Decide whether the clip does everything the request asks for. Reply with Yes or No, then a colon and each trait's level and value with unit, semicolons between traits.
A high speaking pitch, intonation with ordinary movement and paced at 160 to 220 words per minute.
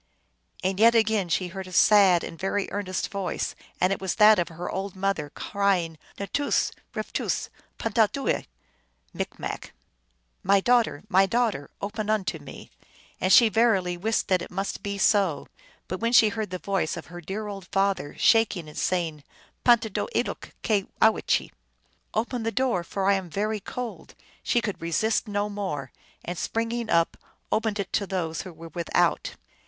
Yes: high, 195 Hz; average, 3.5 semitones; average, 180 wpm